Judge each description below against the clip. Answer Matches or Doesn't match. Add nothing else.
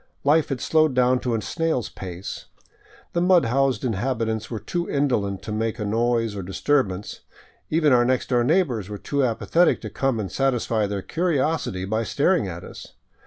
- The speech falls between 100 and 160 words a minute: Doesn't match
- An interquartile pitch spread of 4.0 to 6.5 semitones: Matches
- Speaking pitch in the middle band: Doesn't match